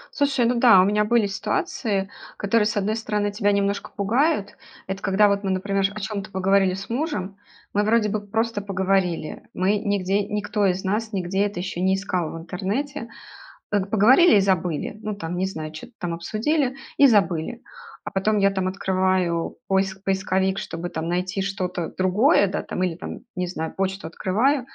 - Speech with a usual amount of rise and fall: No, narrow, 2.2 semitones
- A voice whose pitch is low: No, high, 195 Hz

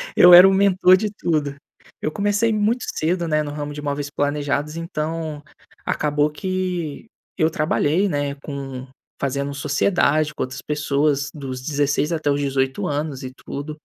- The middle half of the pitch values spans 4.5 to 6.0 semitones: No, average, 3.0 semitones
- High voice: No, medium, 150 Hz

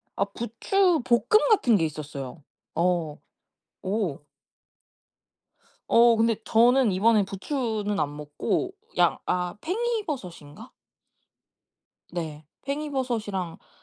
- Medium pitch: No, high, 210 Hz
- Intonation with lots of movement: Yes, wide, 7.2 semitones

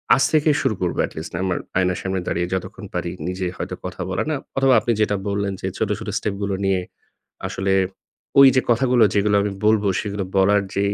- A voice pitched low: Yes, low, 100 Hz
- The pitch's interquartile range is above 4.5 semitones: No, narrow, 2.5 semitones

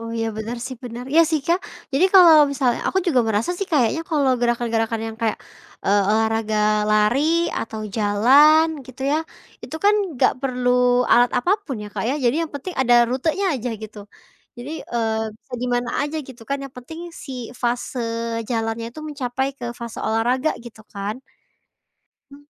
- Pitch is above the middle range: Yes, high, 245 Hz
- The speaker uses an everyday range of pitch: Yes, average, 4.0 semitones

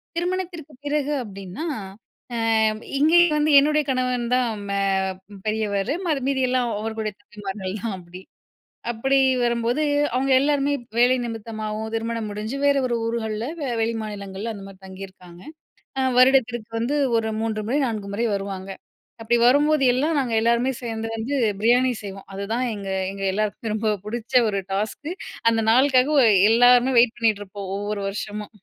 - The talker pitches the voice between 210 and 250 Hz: Yes, high, 230 Hz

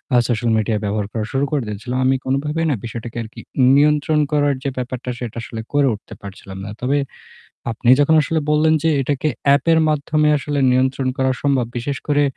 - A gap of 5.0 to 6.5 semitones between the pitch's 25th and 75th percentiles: No, average, 3.6 semitones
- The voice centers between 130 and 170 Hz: Yes, low, 135 Hz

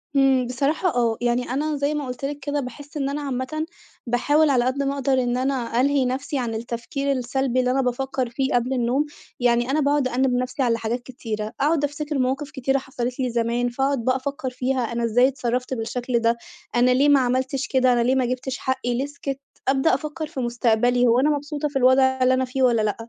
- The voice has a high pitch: Yes, very high, 260 Hz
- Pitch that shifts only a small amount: Yes, narrow, 2.2 semitones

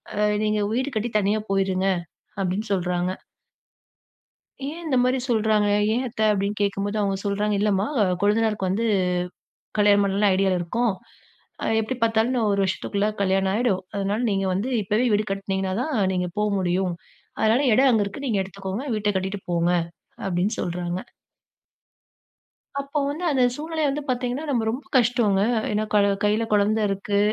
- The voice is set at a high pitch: Yes, high, 205 Hz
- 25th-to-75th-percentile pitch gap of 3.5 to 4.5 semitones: No, average, 3.0 semitones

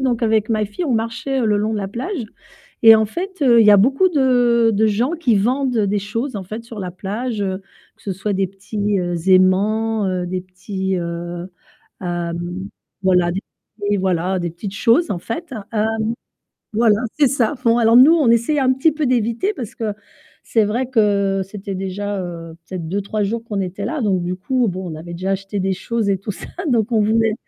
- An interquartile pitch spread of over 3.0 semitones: Yes, average, 3.7 semitones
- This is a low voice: No, high, 210 Hz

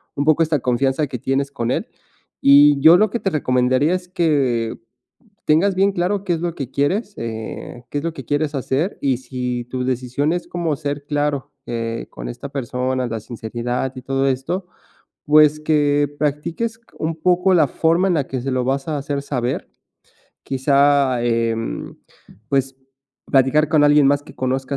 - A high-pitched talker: No, medium, 140 Hz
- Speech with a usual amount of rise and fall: Yes, average, 3.5 semitones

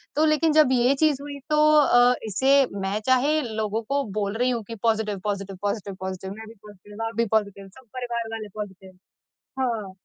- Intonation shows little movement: No, average, 4.3 semitones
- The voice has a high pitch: Yes, high, 225 Hz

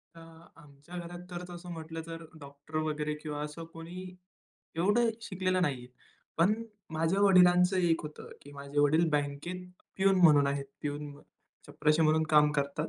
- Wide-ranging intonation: No, average, 3.3 semitones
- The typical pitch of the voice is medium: Yes, medium, 160 Hz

